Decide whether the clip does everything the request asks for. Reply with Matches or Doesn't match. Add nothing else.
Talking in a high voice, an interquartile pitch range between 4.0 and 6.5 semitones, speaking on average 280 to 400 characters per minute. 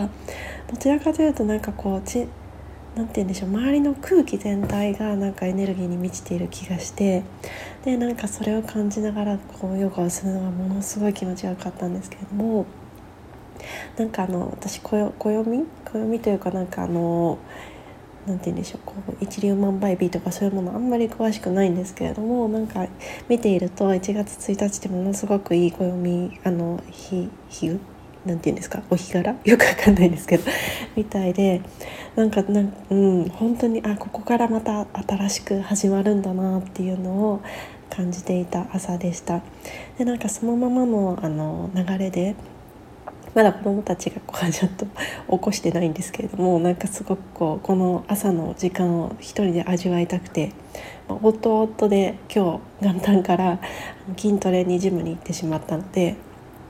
Doesn't match